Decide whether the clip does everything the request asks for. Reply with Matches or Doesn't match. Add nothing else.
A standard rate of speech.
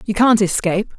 Matches